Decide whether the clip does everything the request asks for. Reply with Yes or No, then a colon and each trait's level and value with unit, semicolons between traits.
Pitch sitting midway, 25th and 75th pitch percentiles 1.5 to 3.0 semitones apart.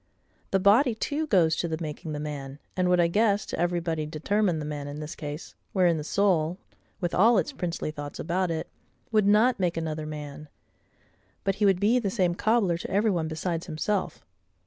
No: medium, 175 Hz; average, 4.5 semitones